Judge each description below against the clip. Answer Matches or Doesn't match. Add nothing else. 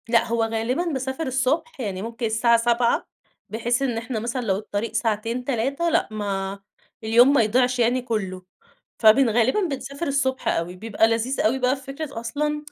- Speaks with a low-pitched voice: Doesn't match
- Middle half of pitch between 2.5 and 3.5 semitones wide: Matches